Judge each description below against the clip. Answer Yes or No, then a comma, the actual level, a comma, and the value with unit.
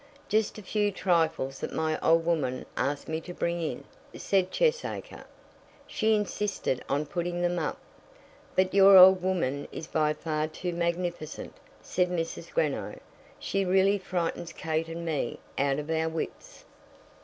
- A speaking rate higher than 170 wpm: No, average, 150 wpm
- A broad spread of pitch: No, average, 3.0 semitones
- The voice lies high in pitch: No, medium, 170 Hz